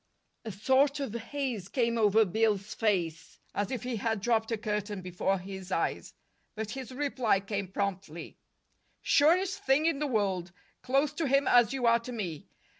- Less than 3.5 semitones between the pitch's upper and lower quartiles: No, average, 5.0 semitones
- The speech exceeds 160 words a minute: Yes, average, 170 wpm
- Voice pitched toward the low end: No, high, 220 Hz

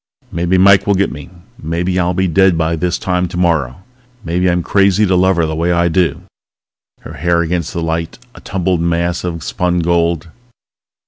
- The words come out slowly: No, average, 185 wpm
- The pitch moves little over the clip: Yes, narrow, 1.6 semitones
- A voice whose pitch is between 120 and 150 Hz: No, very low, 85 Hz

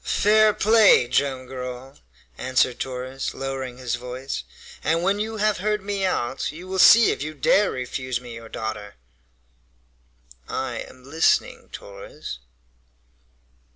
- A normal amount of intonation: No, wide, 7.4 semitones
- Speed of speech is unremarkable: No, slow, 130 wpm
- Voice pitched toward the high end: No, low, 135 Hz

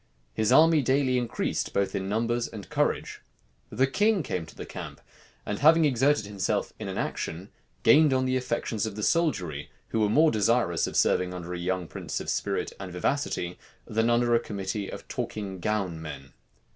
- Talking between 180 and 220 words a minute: Yes, average, 185 wpm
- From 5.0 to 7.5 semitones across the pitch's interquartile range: Yes, wide, 5.5 semitones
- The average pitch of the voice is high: No, low, 110 Hz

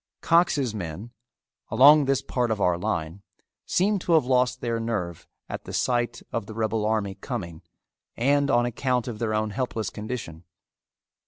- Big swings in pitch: No, average, 3.4 semitones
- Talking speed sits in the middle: Yes, average, 160 wpm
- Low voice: Yes, low, 115 Hz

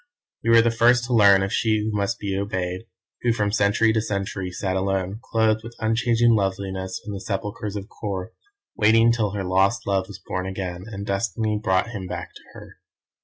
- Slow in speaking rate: No, average, 195 wpm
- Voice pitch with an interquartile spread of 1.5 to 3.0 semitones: Yes, average, 2.7 semitones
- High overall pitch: No, low, 100 Hz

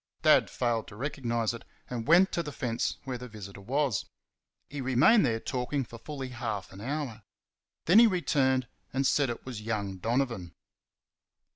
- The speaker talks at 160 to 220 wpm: Yes, average, 165 wpm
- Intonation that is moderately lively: Yes, average, 3.7 semitones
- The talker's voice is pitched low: Yes, low, 125 Hz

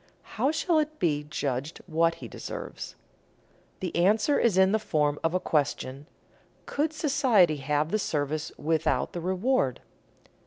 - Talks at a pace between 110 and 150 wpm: Yes, average, 145 wpm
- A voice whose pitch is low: No, medium, 170 Hz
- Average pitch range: No, wide, 6.7 semitones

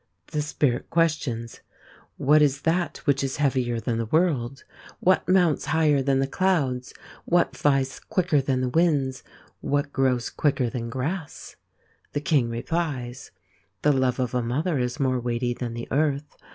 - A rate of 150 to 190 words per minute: Yes, average, 155 wpm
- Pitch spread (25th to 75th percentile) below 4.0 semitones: Yes, average, 3.5 semitones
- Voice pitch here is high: No, low, 135 Hz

